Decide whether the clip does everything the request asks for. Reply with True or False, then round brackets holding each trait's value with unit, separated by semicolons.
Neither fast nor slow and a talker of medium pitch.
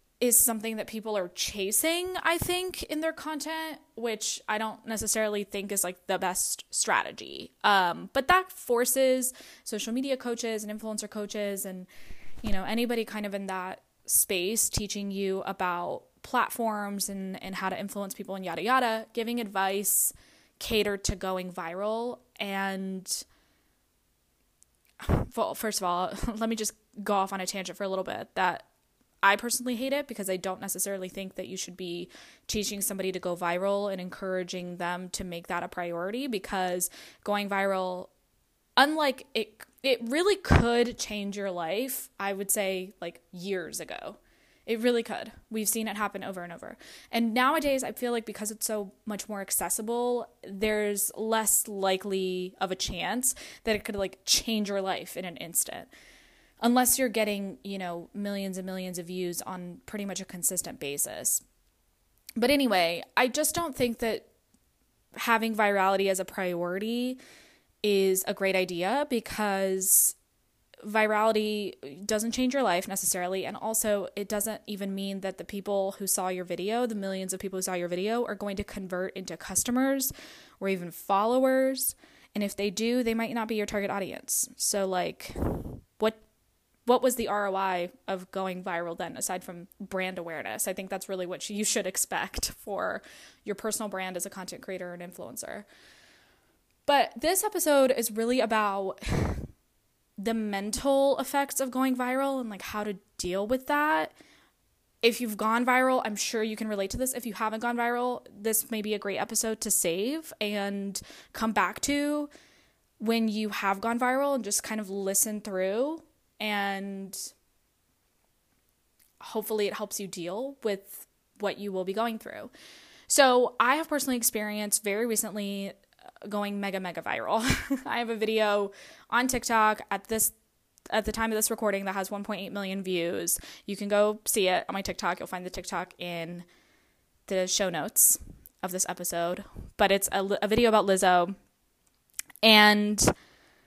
False (165 wpm; 205 Hz)